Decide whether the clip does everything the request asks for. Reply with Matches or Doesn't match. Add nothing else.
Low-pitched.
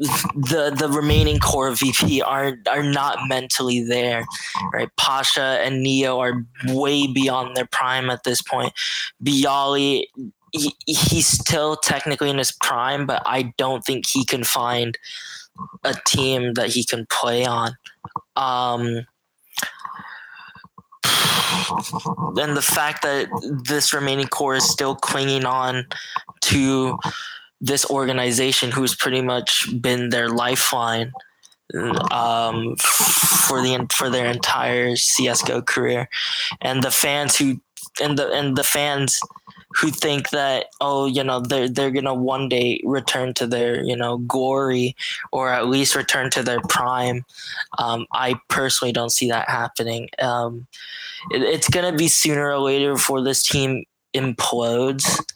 Matches